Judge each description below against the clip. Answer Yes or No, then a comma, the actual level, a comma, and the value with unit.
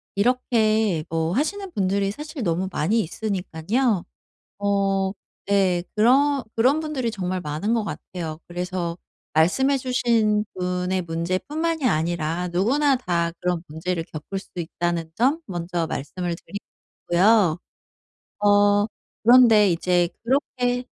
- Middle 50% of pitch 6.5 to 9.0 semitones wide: No, wide, 5.4 semitones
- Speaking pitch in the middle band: No, high, 195 Hz